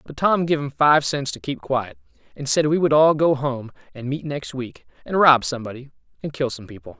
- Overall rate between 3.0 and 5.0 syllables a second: No, 5.4 syllables/s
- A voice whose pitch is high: No, low, 135 Hz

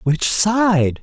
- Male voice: Yes, male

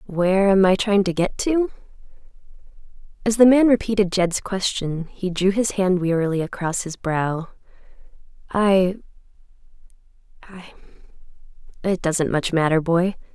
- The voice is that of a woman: Yes, female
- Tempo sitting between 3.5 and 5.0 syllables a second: Yes, 4.7 syllables/s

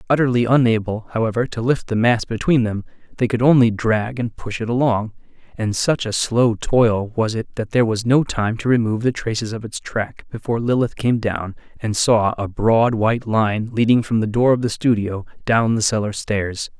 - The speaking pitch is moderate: No, low, 115 Hz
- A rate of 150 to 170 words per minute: No, average, 200 wpm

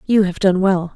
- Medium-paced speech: No, fast, 255 wpm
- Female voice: Yes, female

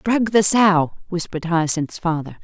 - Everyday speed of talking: Yes, average, 150 wpm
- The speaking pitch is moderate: Yes, medium, 180 Hz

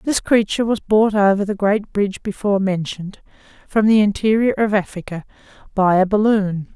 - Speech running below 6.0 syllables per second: Yes, 5.5 syllables/s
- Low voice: No, high, 205 Hz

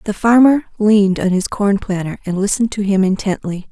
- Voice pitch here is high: Yes, high, 200 Hz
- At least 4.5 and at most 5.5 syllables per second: No, 5.7 syllables/s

